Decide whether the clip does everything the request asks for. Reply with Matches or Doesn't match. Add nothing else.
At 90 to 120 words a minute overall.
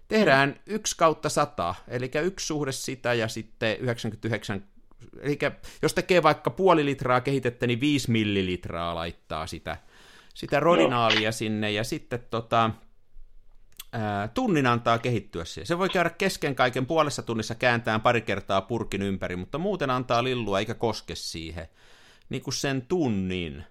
Doesn't match